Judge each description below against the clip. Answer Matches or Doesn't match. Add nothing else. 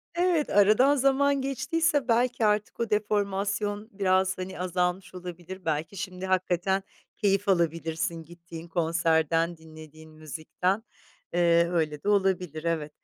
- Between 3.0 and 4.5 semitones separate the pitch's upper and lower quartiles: Matches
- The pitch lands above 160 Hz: Matches